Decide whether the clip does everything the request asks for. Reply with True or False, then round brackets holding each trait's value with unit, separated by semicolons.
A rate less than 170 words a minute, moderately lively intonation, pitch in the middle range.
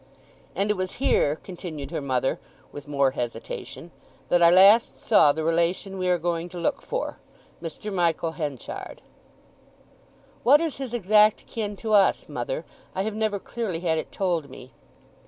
True (155 wpm; 4.8 semitones; 175 Hz)